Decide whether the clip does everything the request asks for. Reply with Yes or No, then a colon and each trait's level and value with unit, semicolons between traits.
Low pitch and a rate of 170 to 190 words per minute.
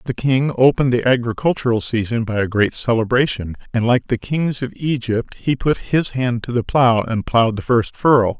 No: low, 120 Hz; average, 200 wpm